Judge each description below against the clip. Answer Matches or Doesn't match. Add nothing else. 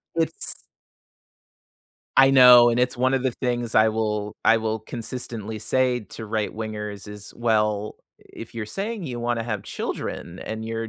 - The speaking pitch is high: Doesn't match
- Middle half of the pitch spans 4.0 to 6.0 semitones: Doesn't match